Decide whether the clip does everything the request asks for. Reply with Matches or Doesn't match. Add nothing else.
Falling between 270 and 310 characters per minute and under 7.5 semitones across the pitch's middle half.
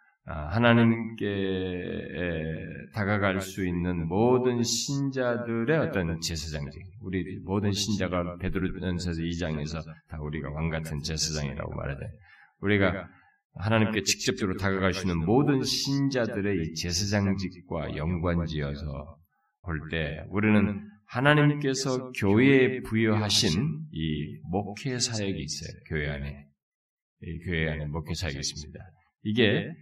Matches